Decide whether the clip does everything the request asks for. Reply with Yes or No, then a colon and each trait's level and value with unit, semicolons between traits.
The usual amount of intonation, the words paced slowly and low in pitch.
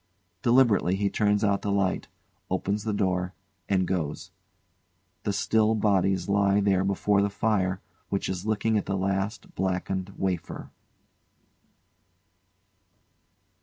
No: narrow, 1.7 semitones; slow, 125 wpm; low, 100 Hz